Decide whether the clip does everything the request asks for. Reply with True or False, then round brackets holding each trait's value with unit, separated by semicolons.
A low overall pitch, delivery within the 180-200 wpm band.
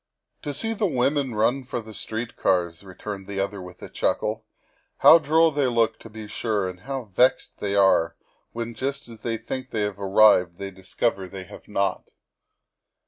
True (110 Hz; 195 wpm)